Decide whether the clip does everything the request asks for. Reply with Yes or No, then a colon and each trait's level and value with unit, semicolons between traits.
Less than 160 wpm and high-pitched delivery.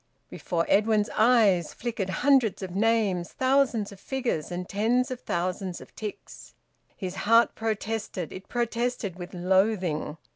Yes: slow, 135 wpm; high, 210 Hz